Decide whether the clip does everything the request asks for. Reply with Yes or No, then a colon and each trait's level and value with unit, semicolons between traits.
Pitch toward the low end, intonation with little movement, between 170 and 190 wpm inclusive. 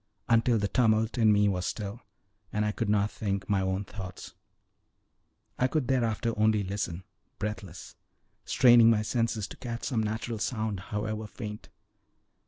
No: low, 110 Hz; narrow, 2.1 semitones; average, 150 wpm